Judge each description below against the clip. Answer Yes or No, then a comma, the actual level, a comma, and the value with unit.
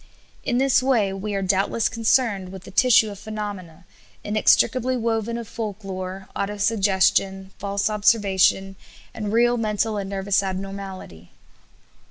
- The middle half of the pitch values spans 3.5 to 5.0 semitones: No, narrow, 2.6 semitones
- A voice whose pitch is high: Yes, high, 200 Hz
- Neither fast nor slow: No, slow, 130 wpm